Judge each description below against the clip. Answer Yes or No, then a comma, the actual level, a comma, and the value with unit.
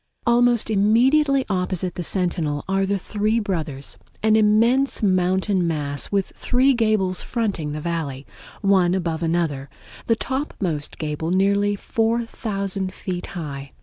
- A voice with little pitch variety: No, average, 4.6 semitones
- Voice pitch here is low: No, high, 190 Hz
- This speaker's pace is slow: Yes, slow, 125 wpm